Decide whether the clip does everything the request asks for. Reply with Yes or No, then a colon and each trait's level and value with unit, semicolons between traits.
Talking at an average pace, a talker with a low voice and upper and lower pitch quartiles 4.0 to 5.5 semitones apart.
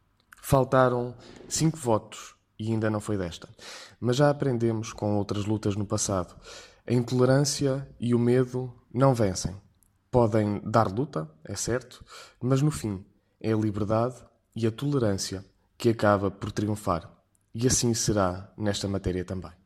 No: average, 145 wpm; low, 110 Hz; average, 3.6 semitones